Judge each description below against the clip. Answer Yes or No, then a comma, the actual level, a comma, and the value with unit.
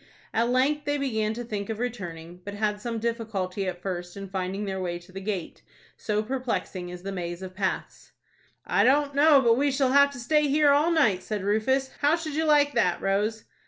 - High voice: Yes, high, 220 Hz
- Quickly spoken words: Yes, fast, 210 wpm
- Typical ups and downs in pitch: No, wide, 6.4 semitones